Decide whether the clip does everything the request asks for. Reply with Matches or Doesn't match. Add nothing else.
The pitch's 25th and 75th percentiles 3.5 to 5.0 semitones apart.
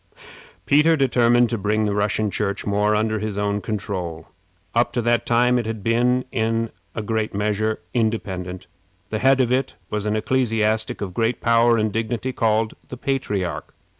Doesn't match